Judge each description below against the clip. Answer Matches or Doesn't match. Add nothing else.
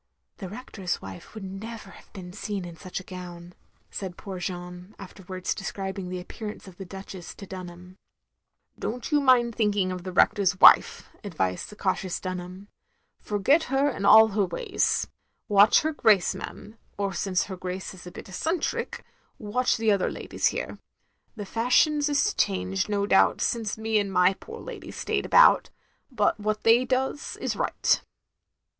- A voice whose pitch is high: Matches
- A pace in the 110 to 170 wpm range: Matches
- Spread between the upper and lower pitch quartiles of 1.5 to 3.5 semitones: Matches